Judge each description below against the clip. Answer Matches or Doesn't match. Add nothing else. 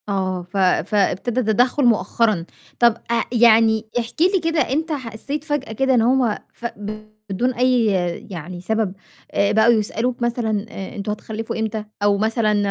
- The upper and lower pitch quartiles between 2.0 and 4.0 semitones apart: Matches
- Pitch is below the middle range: Doesn't match